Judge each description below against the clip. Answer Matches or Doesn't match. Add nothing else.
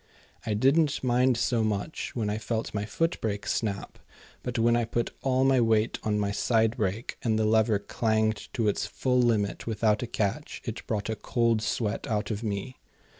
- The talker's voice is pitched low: Matches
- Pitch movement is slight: Matches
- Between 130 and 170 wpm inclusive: Doesn't match